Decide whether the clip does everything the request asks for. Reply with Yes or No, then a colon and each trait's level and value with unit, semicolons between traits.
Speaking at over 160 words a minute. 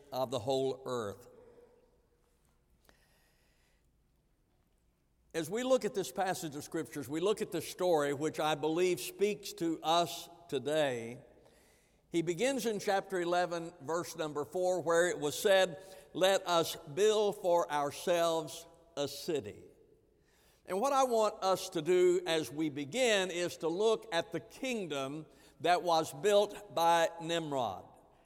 No: slow, 135 wpm